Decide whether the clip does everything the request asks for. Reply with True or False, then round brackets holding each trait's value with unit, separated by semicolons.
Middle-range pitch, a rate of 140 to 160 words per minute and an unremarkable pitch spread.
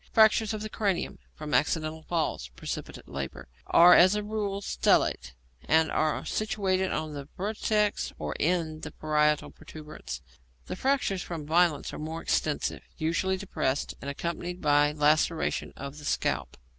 True (160 Hz; 145 wpm; 4.1 semitones)